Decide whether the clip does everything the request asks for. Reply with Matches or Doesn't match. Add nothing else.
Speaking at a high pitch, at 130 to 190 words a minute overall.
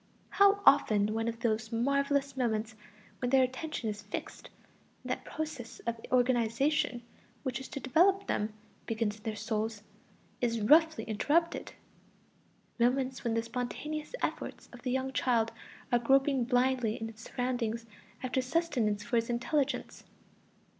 Matches